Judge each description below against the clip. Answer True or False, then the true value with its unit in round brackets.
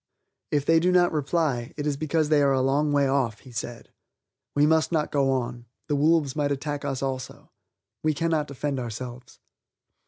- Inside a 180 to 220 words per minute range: True (185 wpm)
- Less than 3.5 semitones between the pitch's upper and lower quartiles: True (2.7 semitones)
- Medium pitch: True (145 Hz)